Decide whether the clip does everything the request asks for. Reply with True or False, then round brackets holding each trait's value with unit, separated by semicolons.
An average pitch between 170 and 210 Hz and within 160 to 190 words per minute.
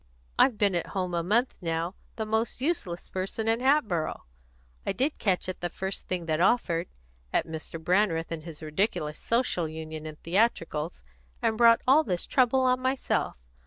True (185 Hz; 170 wpm)